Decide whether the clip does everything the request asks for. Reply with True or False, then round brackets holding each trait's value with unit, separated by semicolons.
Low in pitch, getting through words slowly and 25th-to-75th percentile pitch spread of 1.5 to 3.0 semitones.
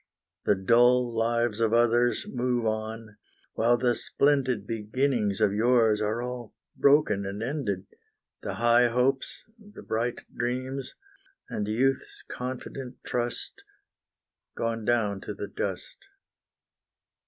True (120 Hz; 115 wpm; 2.5 semitones)